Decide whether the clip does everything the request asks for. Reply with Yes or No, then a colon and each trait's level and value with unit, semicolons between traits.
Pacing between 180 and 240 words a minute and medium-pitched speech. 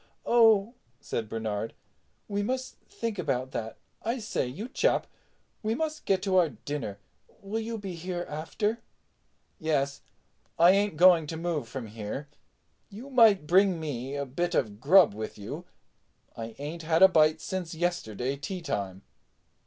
No: average, 145 wpm; medium, 165 Hz